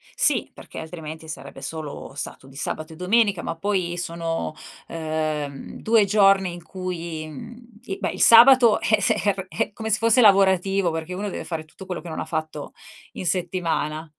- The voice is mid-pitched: Yes, medium, 175 Hz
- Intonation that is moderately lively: Yes, average, 4.1 semitones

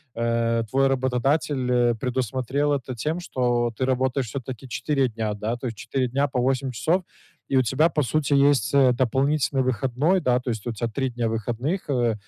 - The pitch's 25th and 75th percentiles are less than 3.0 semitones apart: Yes, narrow, 2.4 semitones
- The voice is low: Yes, low, 130 Hz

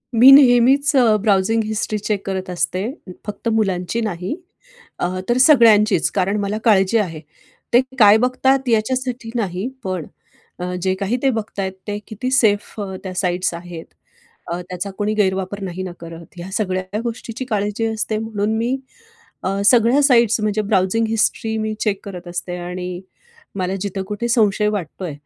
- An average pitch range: Yes, average, 3.3 semitones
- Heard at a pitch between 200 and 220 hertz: Yes, high, 205 Hz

